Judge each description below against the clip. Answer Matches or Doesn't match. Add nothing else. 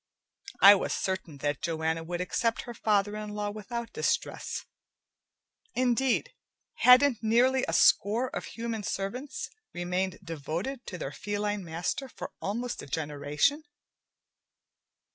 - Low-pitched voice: Doesn't match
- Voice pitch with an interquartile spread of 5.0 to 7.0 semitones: Matches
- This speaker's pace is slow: Matches